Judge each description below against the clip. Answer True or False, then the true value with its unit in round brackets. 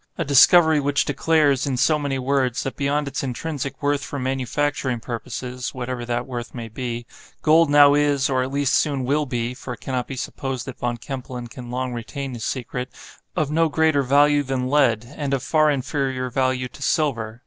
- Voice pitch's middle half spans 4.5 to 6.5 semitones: False (2.5 semitones)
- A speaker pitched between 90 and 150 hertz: True (135 Hz)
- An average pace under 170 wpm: False (190 wpm)